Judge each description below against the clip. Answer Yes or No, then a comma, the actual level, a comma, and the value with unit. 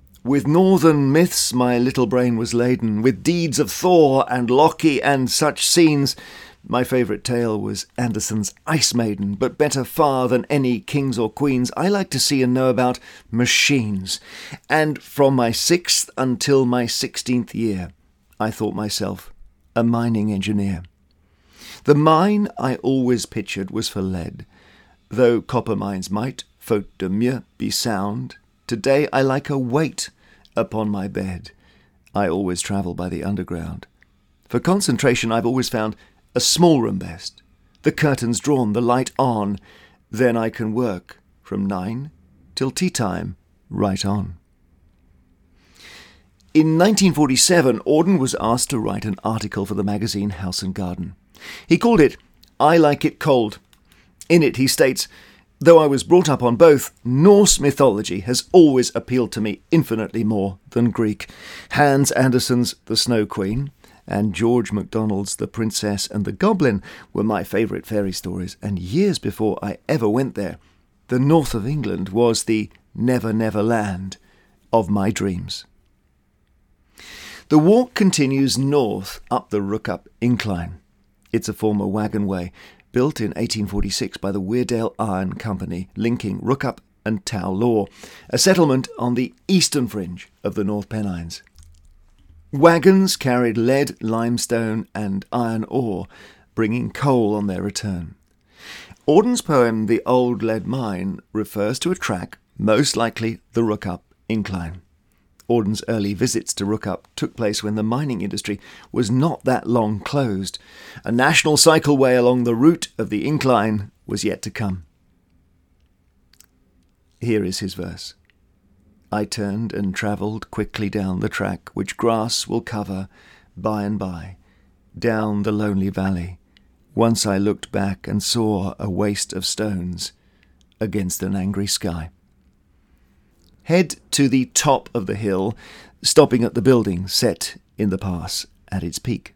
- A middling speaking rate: Yes, average, 145 wpm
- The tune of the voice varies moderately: Yes, average, 4.7 semitones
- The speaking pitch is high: No, low, 110 Hz